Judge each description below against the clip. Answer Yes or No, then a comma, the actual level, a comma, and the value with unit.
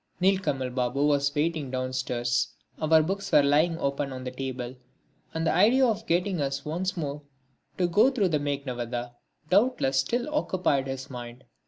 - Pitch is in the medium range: Yes, medium, 145 Hz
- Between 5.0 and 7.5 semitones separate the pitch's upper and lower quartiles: Yes, wide, 5.6 semitones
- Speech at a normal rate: Yes, average, 160 wpm